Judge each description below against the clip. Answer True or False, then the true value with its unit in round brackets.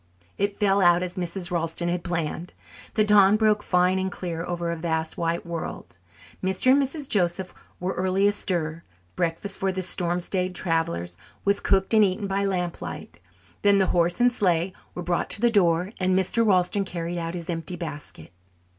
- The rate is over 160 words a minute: True (180 wpm)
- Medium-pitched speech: True (180 Hz)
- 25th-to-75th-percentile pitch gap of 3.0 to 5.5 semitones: False (2.6 semitones)